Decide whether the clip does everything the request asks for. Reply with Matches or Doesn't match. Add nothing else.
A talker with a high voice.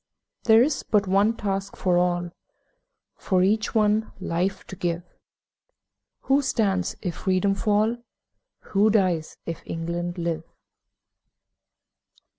Matches